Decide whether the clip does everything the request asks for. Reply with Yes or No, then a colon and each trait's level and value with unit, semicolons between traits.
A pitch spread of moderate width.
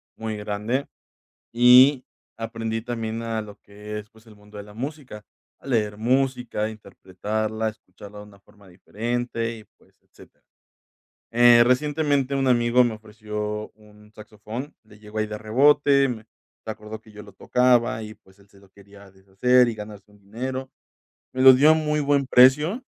Yes: average, 3.1 semitones